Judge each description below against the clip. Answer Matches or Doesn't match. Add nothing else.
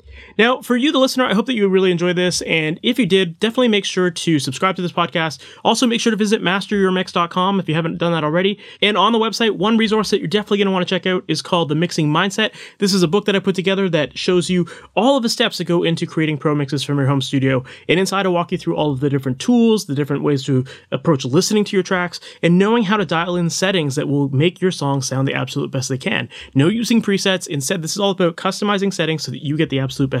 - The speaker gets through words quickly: Matches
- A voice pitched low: Doesn't match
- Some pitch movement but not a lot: Matches